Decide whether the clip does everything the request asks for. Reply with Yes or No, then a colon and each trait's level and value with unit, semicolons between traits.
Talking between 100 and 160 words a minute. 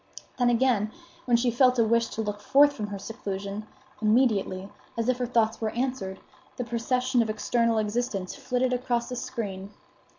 No: average, 170 wpm